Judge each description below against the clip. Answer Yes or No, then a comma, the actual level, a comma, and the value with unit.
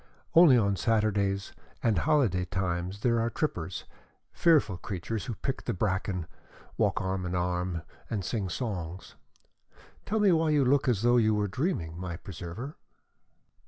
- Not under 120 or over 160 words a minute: Yes, average, 150 wpm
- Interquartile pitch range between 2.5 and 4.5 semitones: No, average, 5.2 semitones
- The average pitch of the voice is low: Yes, low, 100 Hz